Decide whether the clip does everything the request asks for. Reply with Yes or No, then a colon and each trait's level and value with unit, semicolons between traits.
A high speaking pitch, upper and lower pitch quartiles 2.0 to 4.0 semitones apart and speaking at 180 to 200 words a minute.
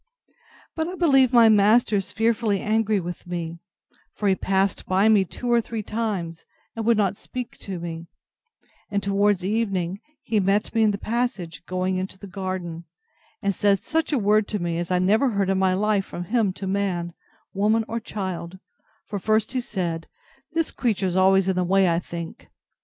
Yes: high, 200 Hz; average, 3.1 semitones; average, 185 wpm